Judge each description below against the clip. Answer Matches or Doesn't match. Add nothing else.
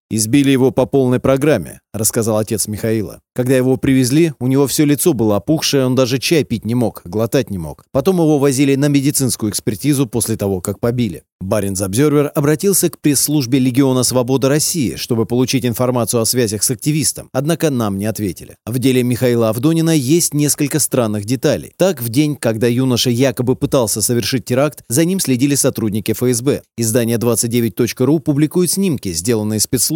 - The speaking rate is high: Matches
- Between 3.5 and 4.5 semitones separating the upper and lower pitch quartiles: Matches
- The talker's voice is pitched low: Matches